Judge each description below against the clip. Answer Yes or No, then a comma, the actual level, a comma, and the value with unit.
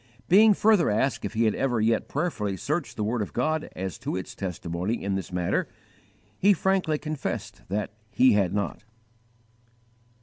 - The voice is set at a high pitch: No, low, 115 Hz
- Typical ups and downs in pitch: No, wide, 7.9 semitones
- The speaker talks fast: No, average, 165 wpm